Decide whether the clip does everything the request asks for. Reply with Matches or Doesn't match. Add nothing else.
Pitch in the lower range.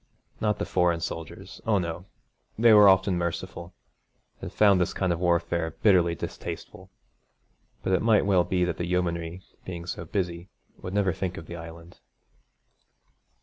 Matches